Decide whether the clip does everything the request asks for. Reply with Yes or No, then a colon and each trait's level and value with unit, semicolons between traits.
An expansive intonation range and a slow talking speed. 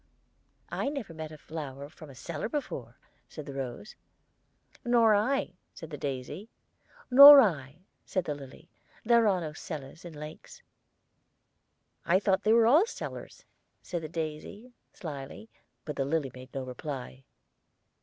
No: wide, 7.7 semitones; average, 145 wpm